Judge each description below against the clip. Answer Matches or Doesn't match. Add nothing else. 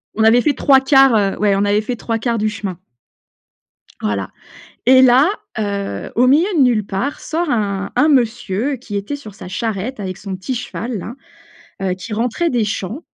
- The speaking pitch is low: Doesn't match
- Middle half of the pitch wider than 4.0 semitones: Matches